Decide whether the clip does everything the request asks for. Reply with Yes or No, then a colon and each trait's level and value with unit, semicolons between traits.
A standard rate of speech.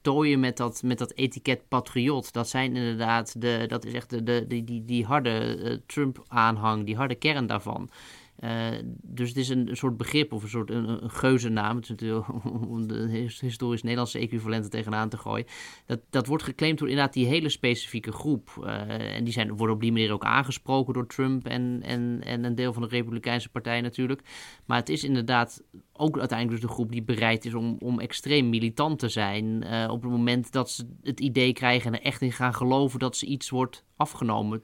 No: fast, 205 wpm